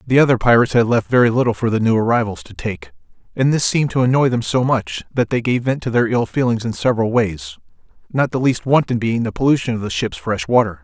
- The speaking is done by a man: Yes, male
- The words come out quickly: Yes, fast, 245 wpm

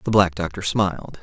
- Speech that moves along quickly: No, average, 195 wpm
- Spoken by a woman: No, male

